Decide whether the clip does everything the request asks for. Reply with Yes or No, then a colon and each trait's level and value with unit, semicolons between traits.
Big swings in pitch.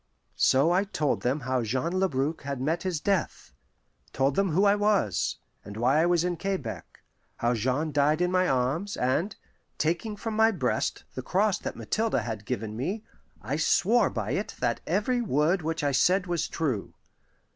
Yes: wide, 6.6 semitones